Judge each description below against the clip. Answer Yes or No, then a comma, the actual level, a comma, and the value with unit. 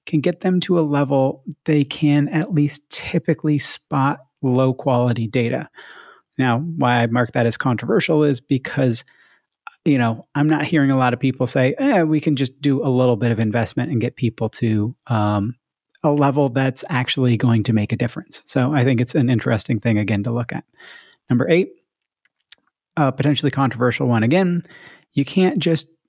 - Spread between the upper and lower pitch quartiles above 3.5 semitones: Yes, average, 4.1 semitones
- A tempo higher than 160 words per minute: Yes, average, 180 wpm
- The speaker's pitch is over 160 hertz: No, low, 135 Hz